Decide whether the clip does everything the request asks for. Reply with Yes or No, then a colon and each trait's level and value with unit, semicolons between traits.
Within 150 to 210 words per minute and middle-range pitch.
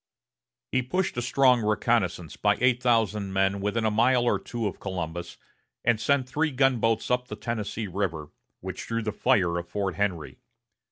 No: average, 170 wpm; low, 110 Hz